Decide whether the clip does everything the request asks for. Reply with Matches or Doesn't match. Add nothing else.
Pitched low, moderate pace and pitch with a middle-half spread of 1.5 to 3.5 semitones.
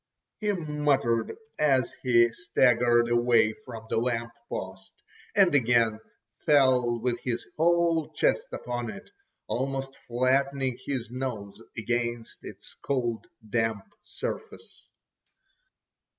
Doesn't match